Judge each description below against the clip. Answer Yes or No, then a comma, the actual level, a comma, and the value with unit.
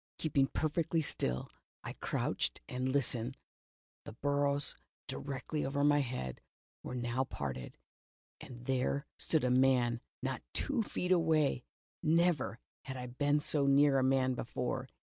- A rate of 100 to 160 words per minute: Yes, slow, 135 wpm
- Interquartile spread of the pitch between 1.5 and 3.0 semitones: Yes, average, 2.7 semitones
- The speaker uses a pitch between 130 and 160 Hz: Yes, low, 135 Hz